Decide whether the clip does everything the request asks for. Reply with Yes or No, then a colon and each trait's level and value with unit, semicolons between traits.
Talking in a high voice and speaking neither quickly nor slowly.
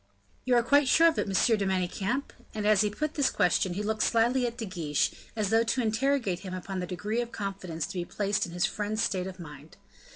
No: high, 205 Hz; fast, 235 wpm